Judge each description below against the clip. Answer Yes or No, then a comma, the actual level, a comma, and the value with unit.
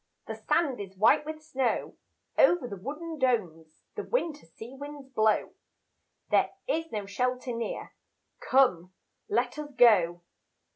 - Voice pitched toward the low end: No, very high, 250 Hz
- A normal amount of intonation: No, wide, 6.6 semitones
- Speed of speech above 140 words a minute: No, slow, 135 wpm